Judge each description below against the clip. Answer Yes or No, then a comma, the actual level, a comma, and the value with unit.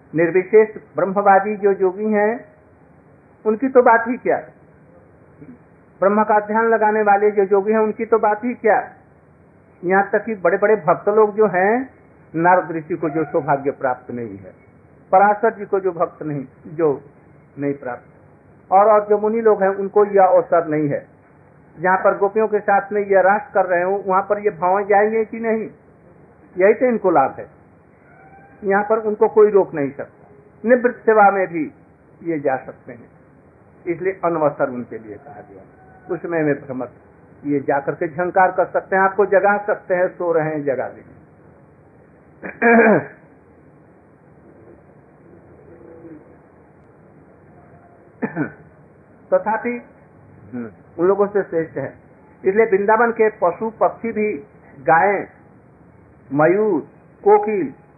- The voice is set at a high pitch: Yes, high, 195 Hz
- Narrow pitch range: No, average, 4.8 semitones